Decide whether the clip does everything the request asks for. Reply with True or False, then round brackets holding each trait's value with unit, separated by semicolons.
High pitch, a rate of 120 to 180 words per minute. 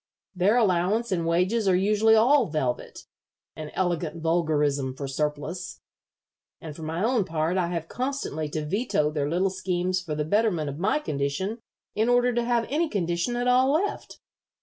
False (180 Hz; 170 wpm)